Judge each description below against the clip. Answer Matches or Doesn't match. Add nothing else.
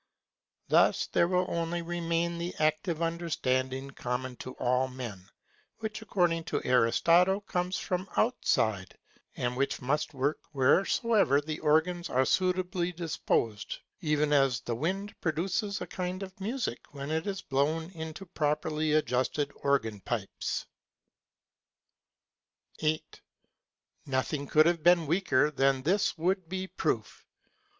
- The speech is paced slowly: Matches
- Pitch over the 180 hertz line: Doesn't match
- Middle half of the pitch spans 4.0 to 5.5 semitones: Matches